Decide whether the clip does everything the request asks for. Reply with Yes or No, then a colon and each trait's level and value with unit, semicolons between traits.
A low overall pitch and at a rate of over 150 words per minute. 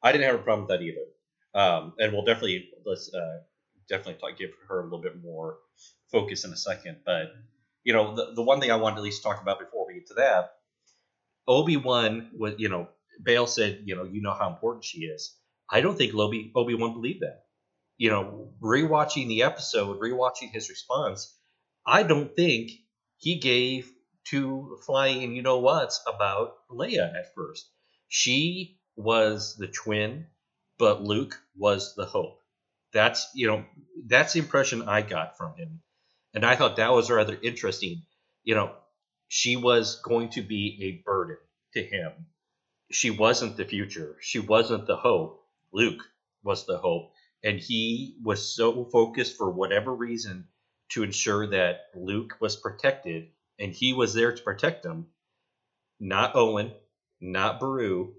Yes: low, 120 Hz; average, 165 wpm